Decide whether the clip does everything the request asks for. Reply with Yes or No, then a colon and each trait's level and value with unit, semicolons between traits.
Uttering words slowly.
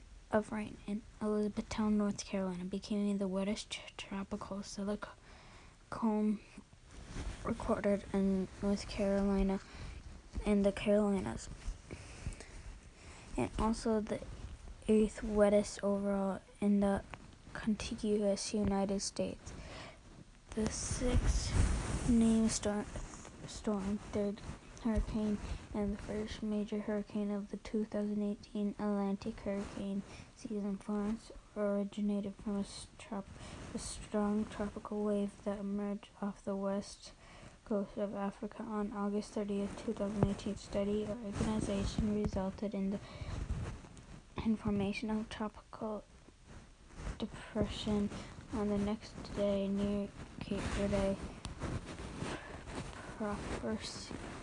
Yes: slow, 95 wpm